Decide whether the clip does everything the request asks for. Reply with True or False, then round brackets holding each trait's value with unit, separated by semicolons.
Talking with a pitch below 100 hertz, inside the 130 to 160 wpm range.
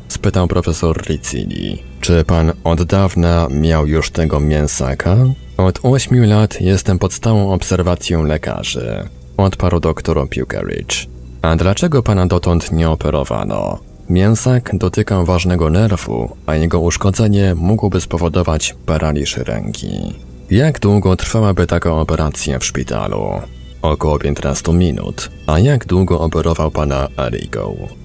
False (85 Hz; 120 wpm)